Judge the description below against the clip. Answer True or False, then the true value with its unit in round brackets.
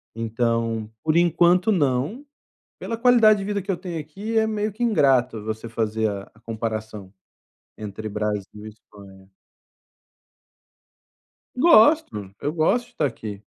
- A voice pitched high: False (125 Hz)